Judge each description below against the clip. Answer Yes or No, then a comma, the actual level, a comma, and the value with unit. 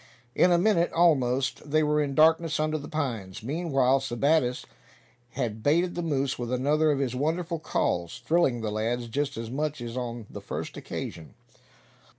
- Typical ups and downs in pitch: Yes, average, 4.4 semitones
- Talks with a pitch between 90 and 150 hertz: Yes, medium, 140 Hz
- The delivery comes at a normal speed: Yes, average, 165 wpm